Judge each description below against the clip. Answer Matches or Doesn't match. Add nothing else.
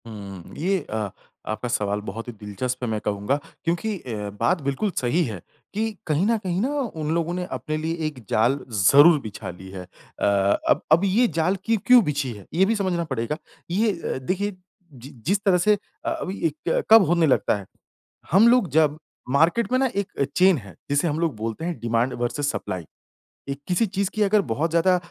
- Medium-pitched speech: Matches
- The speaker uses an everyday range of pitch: Doesn't match